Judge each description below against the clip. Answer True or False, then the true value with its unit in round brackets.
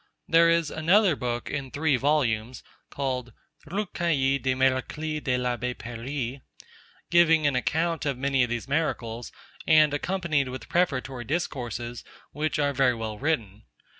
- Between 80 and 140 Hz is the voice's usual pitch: True (135 Hz)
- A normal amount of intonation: True (4.1 semitones)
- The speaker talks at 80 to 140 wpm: True (135 wpm)